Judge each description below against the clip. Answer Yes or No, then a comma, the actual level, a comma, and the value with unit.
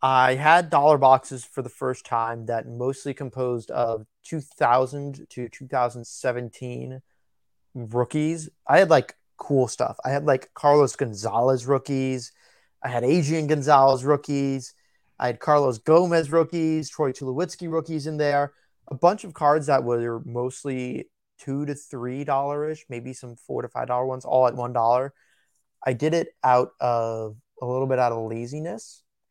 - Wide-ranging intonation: No, average, 3.1 semitones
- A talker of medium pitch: No, low, 130 Hz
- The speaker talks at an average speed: Yes, average, 160 wpm